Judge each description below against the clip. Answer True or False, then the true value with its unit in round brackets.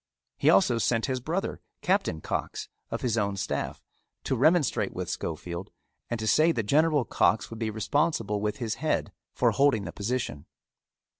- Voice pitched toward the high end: False (115 Hz)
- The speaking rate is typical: True (165 wpm)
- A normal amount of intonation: False (5.9 semitones)